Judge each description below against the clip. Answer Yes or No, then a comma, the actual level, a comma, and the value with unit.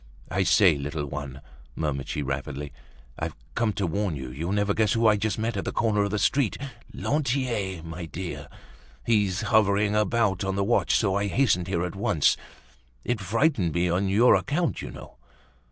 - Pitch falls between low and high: No, low, 100 Hz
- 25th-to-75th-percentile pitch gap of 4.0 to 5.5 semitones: Yes, average, 4.4 semitones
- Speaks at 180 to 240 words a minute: Yes, average, 185 wpm